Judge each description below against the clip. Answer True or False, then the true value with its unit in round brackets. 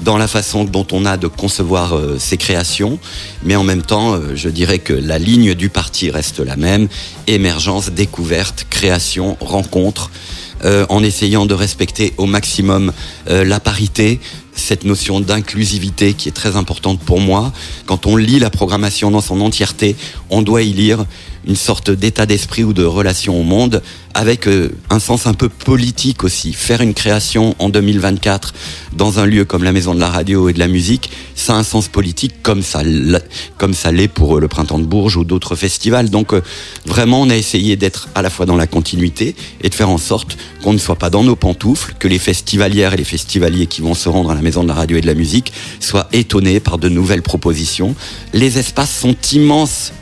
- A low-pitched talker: True (100 Hz)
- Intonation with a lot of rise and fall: False (3.2 semitones)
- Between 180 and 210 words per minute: True (200 wpm)